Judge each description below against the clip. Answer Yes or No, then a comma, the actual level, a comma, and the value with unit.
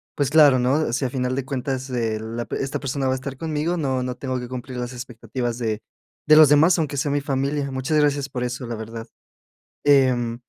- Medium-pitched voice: No, low, 130 Hz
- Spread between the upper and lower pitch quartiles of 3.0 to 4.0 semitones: No, narrow, 2.6 semitones